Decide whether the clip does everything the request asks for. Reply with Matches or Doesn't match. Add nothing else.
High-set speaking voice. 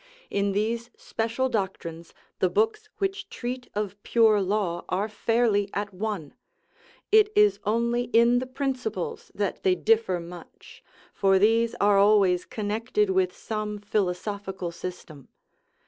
Matches